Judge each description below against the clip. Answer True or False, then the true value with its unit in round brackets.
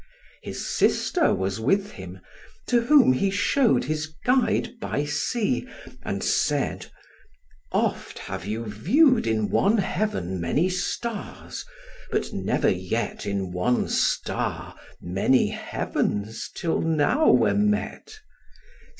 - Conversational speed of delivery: False (115 wpm)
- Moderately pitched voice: True (155 Hz)